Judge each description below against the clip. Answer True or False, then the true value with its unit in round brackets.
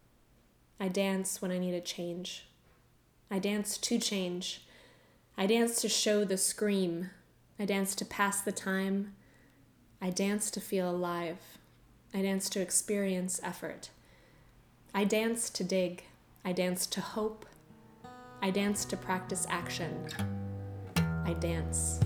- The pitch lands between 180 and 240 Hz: True (190 Hz)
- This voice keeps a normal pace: False (130 wpm)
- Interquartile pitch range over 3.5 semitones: True (4.6 semitones)